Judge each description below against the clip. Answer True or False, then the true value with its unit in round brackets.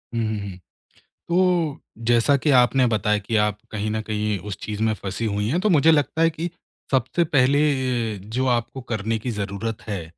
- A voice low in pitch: True (115 Hz)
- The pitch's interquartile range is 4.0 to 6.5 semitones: True (4.7 semitones)